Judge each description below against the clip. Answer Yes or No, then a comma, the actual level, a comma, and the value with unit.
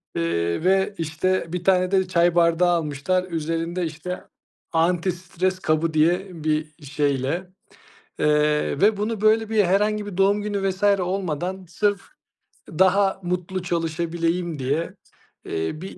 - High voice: No, medium, 175 Hz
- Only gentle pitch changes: No, average, 3.2 semitones